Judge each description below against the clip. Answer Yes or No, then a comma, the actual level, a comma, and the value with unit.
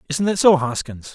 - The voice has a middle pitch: Yes, medium, 155 Hz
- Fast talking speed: Yes, fast, 210 wpm